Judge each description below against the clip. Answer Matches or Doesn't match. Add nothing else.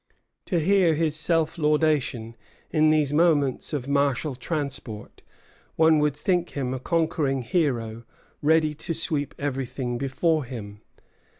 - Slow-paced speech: Matches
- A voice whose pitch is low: Doesn't match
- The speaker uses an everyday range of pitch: Matches